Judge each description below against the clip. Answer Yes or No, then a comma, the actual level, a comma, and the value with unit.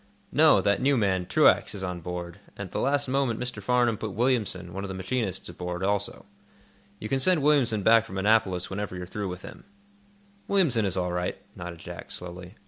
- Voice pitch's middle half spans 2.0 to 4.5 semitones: No, average, 5.0 semitones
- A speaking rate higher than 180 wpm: Yes, average, 200 wpm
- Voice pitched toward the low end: Yes, low, 100 Hz